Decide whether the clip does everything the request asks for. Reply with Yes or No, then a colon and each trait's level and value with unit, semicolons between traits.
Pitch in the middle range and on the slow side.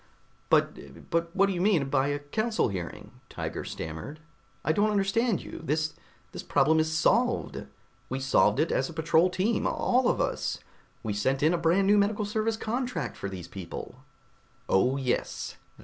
No: medium, 160 Hz; average, 170 wpm